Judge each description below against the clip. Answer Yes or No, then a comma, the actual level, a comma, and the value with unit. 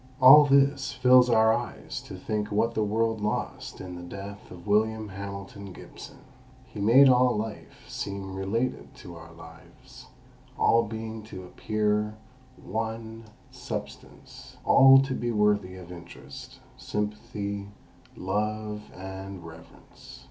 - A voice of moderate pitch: No, low, 105 Hz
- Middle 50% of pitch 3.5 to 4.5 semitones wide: No, average, 2.9 semitones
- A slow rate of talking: Yes, slow, 125 wpm